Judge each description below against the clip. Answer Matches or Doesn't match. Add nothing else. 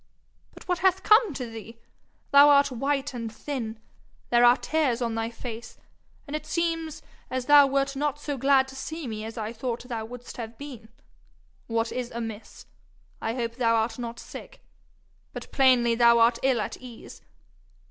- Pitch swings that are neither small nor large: Matches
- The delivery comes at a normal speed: Matches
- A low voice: Doesn't match